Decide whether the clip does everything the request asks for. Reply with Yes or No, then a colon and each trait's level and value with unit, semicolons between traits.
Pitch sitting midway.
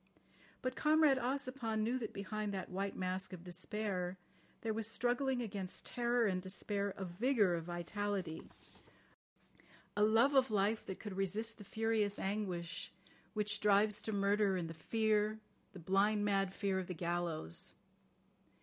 No: high, 205 Hz